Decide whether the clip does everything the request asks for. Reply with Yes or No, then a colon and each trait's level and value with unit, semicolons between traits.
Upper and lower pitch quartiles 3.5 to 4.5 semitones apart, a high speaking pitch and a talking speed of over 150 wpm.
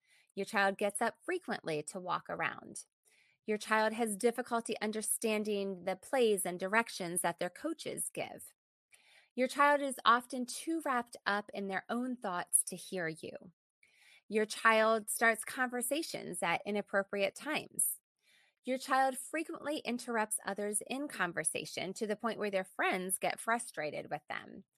No: average, 4.2 semitones; high, 220 Hz; average, 145 wpm